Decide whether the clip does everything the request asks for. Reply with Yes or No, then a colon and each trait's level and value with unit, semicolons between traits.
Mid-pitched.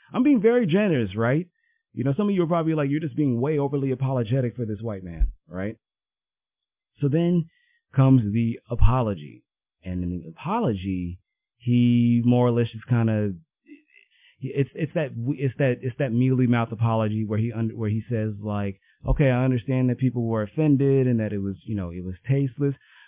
No: low, 120 Hz